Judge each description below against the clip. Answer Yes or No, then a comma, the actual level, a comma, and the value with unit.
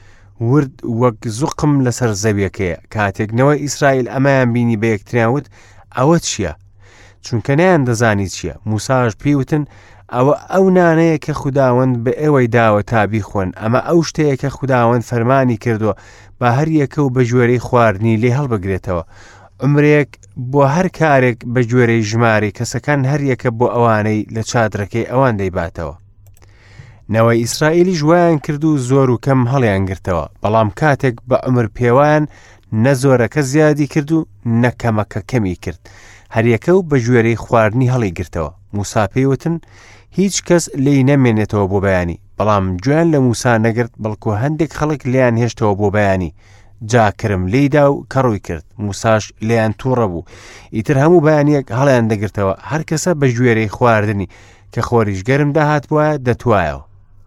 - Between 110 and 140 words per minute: Yes, slow, 135 wpm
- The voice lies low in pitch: Yes, low, 120 Hz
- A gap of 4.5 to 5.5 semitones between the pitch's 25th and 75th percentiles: Yes, average, 5.1 semitones